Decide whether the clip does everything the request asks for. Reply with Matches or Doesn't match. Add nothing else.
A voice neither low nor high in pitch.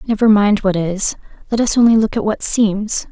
Doesn't match